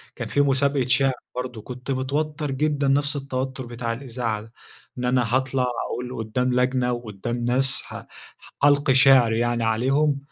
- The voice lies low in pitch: Yes, low, 130 Hz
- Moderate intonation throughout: No, narrow, 2.3 semitones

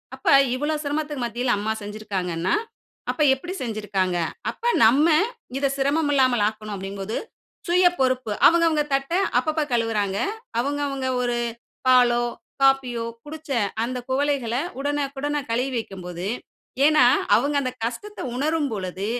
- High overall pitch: Yes, very high, 255 Hz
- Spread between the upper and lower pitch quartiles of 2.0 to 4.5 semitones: No, average, 5.1 semitones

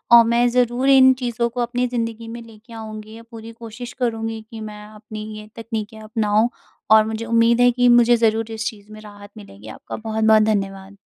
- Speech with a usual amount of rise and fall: No, narrow, 1.6 semitones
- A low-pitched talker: No, high, 225 Hz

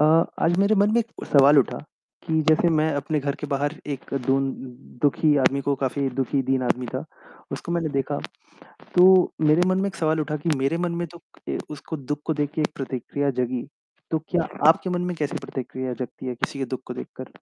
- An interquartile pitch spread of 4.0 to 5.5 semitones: No, average, 3.2 semitones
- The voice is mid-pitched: Yes, medium, 145 Hz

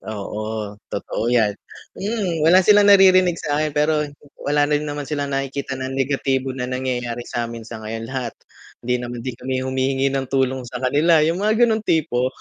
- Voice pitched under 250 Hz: Yes, low, 135 Hz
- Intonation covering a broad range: No, average, 3.9 semitones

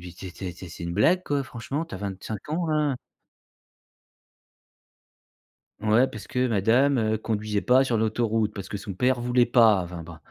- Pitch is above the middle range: No, low, 110 Hz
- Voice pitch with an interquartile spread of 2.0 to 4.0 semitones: No, average, 4.5 semitones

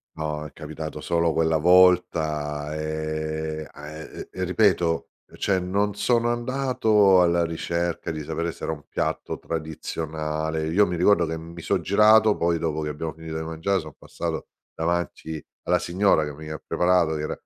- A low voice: Yes, very low, 80 Hz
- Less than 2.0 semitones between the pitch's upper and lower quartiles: No, average, 2.8 semitones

